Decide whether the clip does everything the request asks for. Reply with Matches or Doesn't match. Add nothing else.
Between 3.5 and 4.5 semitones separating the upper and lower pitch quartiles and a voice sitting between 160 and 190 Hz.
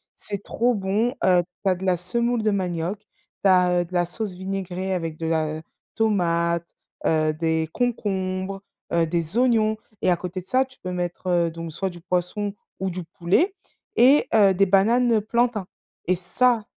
Matches